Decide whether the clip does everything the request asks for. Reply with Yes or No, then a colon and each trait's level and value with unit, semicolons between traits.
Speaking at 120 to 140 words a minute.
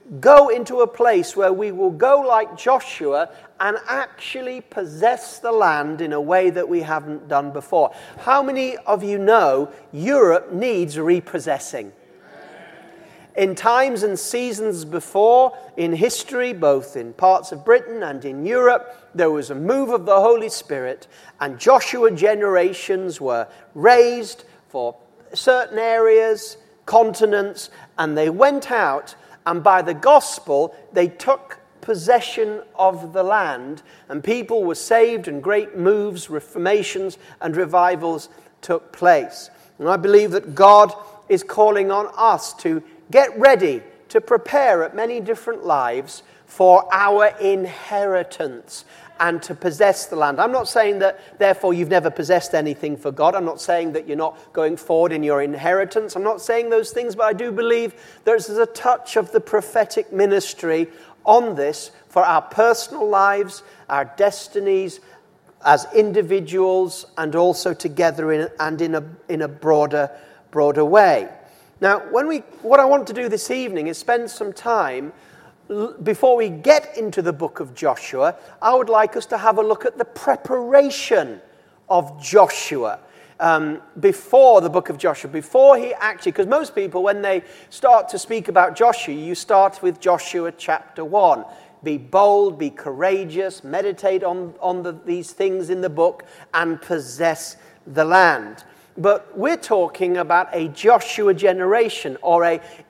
No: average, 150 wpm